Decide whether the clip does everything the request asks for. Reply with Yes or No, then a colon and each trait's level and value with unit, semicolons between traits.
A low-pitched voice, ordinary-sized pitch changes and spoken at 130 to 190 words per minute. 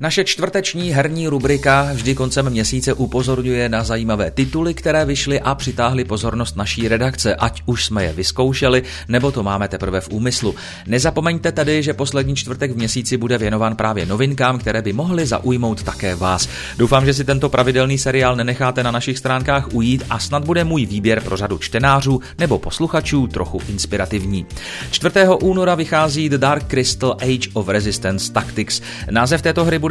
Yes: low, 125 Hz; average, 4.3 semitones; average, 165 wpm